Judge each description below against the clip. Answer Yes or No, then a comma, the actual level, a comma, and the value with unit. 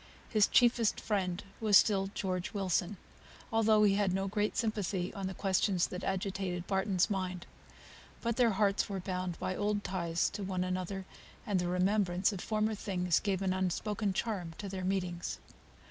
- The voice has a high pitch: Yes, high, 195 Hz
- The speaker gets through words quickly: No, average, 165 wpm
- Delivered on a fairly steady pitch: Yes, narrow, 2.2 semitones